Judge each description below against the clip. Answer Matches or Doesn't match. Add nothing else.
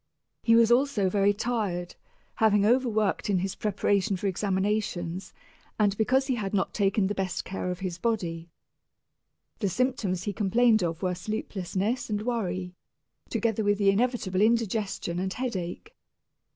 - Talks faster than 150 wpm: Doesn't match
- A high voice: Matches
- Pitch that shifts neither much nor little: Matches